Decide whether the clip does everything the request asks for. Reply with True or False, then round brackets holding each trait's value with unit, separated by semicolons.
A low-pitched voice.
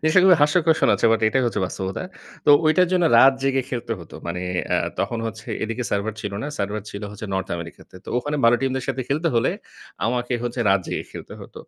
True (120 Hz)